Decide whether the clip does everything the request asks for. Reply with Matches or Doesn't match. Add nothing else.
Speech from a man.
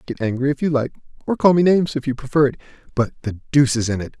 Matches